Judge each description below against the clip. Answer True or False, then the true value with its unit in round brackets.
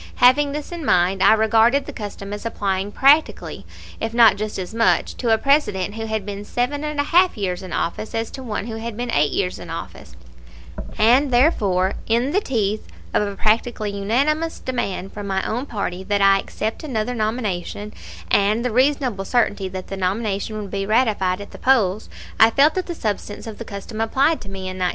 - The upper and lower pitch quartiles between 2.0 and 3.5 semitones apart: False (3.9 semitones)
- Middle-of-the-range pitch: False (220 Hz)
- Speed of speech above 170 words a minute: True (200 wpm)